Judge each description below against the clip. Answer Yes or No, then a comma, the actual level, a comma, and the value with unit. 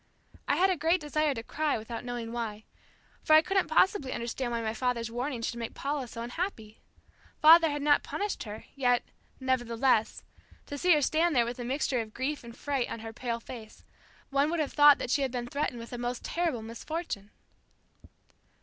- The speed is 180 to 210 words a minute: Yes, average, 195 wpm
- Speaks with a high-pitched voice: Yes, very high, 255 Hz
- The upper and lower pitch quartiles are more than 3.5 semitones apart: Yes, average, 4.3 semitones